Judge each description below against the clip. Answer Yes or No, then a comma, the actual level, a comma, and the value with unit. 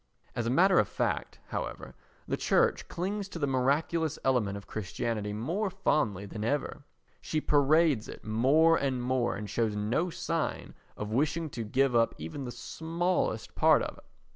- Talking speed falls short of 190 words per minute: Yes, average, 165 wpm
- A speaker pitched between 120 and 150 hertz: Yes, low, 135 Hz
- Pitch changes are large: Yes, wide, 6.6 semitones